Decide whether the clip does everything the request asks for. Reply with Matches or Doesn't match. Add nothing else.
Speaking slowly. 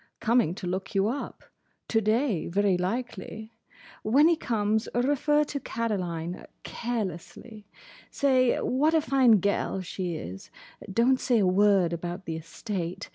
Matches